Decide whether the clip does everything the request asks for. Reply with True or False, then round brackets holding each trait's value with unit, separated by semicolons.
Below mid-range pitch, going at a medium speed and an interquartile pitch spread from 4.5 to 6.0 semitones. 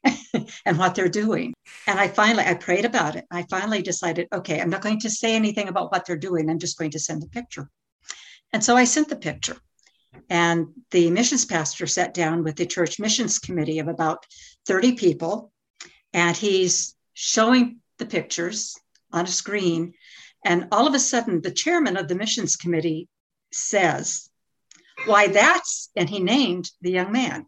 False (185 Hz; 175 wpm; 4.8 semitones)